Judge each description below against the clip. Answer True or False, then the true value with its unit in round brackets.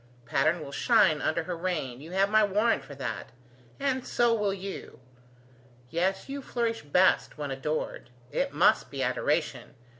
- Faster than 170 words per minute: False (155 wpm)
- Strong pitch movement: True (6.3 semitones)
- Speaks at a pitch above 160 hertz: True (185 Hz)